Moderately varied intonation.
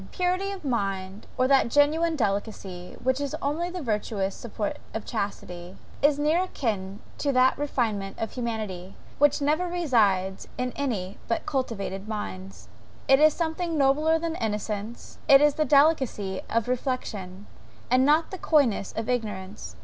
No: wide, 6.5 semitones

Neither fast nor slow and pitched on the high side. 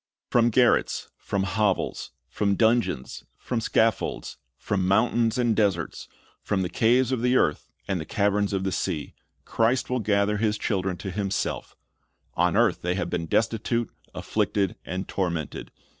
No: average, 155 wpm; low, 105 Hz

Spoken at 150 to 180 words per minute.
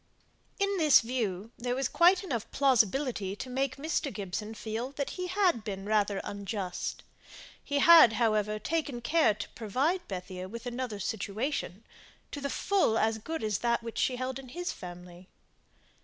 Yes: average, 160 wpm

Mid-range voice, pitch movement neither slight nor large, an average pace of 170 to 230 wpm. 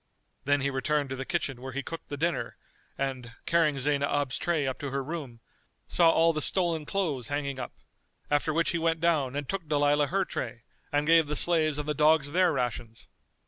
Yes: medium, 145 Hz; average, 3.2 semitones; average, 200 wpm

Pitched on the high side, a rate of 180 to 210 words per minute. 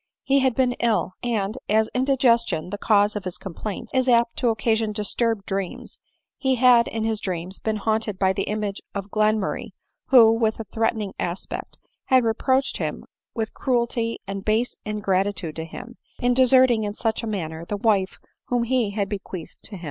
Yes: high, 220 Hz; average, 185 wpm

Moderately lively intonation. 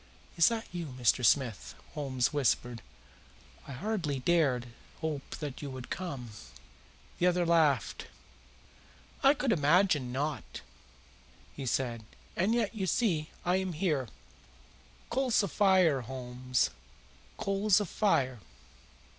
No: wide, 6.4 semitones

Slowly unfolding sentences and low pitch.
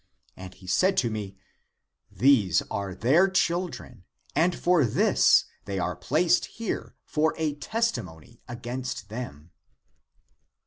Yes: slow, 120 wpm; low, 125 Hz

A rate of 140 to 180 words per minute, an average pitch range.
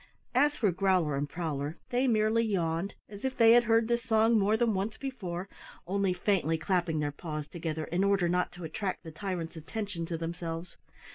No: average, 190 wpm; average, 5.0 semitones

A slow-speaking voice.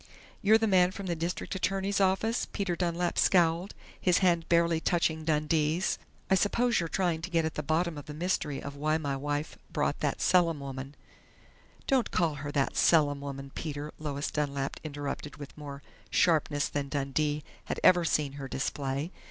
No: average, 175 wpm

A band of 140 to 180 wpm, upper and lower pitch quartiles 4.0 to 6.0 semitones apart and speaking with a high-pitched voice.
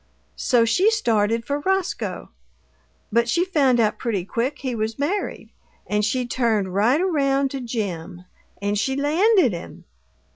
Yes: average, 145 wpm; average, 5.1 semitones; high, 245 Hz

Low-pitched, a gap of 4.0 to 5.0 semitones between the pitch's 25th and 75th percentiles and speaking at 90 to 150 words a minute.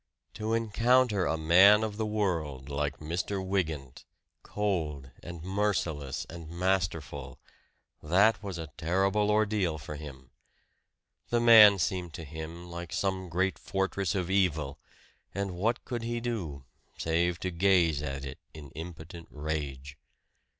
Yes: very low, 85 Hz; average, 4.4 semitones; slow, 135 wpm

